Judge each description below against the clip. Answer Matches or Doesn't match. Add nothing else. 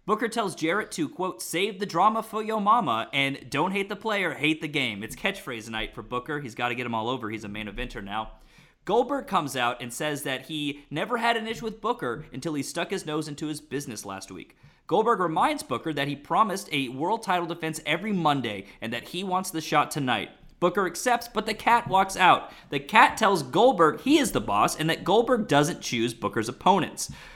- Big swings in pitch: Matches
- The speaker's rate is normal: Doesn't match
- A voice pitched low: Doesn't match